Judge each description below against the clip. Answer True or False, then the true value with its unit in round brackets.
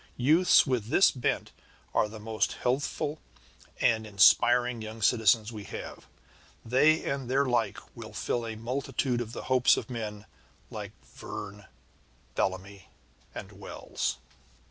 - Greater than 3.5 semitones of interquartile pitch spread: False (3.2 semitones)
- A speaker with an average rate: False (130 wpm)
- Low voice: True (115 Hz)